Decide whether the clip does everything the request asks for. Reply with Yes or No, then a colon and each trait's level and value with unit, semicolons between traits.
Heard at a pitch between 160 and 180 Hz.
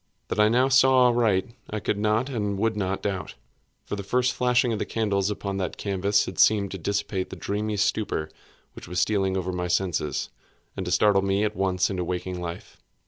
No: low, 100 Hz